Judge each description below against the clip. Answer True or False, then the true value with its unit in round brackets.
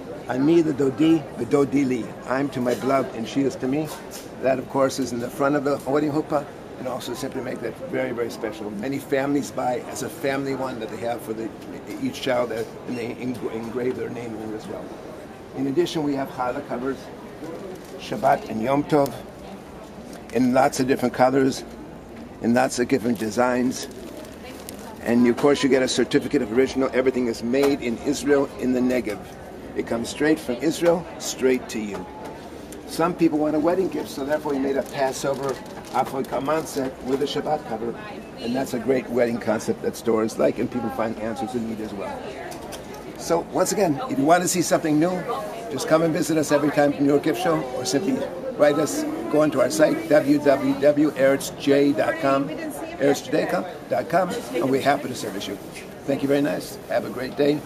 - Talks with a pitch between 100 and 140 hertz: True (135 Hz)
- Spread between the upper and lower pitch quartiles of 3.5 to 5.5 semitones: False (3.0 semitones)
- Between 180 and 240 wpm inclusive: True (190 wpm)